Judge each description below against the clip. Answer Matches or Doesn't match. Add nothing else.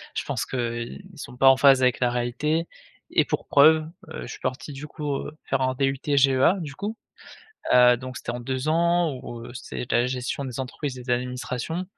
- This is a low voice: Matches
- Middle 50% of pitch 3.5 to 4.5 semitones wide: Doesn't match